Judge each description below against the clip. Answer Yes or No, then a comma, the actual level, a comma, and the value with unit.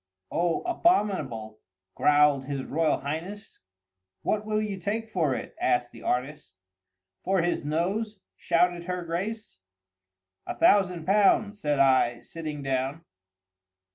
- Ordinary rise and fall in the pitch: No, wide, 6.4 semitones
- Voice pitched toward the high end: No, medium, 170 Hz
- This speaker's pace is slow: Yes, slow, 120 wpm